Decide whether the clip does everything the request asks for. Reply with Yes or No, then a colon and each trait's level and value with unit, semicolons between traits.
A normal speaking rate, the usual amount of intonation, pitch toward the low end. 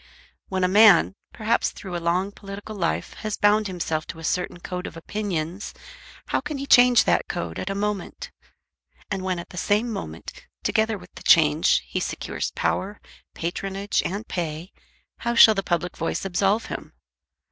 No: average, 170 wpm; average, 3.4 semitones; high, 195 Hz